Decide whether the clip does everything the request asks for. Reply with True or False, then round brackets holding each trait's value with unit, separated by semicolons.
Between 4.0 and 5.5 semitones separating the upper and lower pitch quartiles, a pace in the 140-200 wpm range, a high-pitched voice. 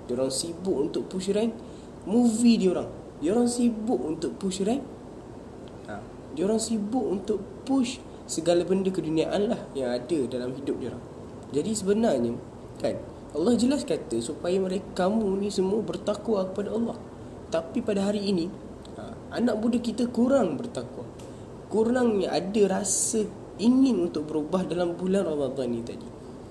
True (5.2 semitones; 150 wpm; 195 Hz)